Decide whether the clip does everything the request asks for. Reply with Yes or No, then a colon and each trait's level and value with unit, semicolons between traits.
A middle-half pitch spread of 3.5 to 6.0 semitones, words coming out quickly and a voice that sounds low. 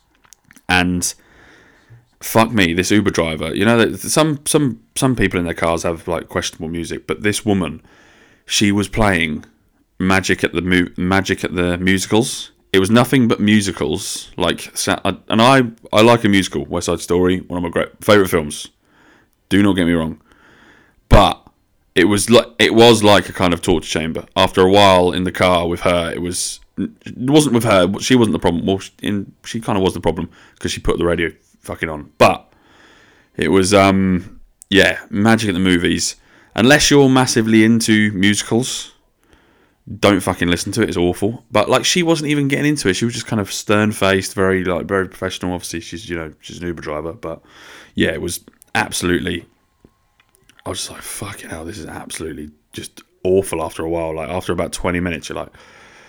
No: average, 4.0 semitones; average, 190 wpm; very low, 95 Hz